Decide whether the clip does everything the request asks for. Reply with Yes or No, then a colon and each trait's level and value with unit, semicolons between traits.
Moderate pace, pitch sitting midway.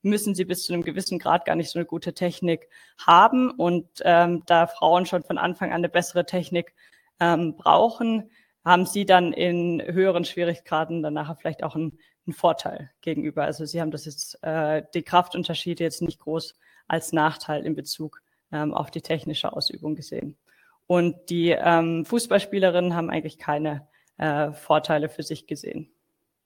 Yes: average, 165 wpm; medium, 170 Hz